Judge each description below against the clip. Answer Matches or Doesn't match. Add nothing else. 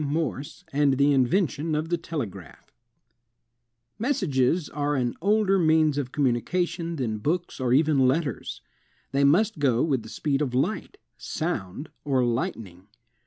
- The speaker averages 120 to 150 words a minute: Matches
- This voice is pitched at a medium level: Matches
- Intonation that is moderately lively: Matches